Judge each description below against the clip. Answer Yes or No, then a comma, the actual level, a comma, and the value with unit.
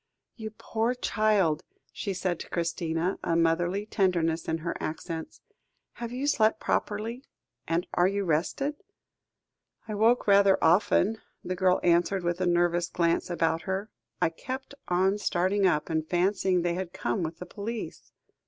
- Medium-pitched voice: Yes, medium, 180 Hz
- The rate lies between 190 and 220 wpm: No, average, 155 wpm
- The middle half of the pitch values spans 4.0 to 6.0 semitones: No, average, 3.4 semitones